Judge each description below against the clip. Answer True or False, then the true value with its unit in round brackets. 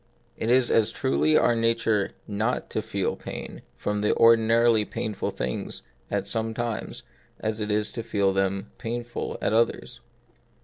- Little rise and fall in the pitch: True (2.1 semitones)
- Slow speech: False (150 wpm)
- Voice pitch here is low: True (110 Hz)